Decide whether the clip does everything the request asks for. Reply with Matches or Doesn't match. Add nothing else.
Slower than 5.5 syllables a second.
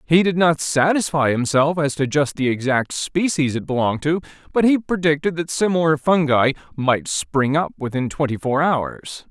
Matches